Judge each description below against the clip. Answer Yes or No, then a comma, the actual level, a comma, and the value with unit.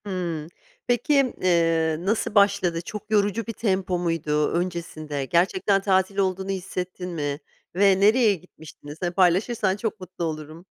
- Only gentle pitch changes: No, average, 3.2 semitones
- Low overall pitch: No, medium, 185 Hz